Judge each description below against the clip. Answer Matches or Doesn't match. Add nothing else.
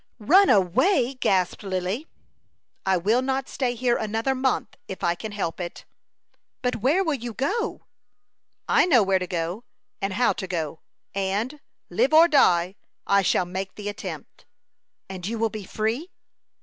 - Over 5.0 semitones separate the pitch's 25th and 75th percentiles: Matches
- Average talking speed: Matches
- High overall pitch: Matches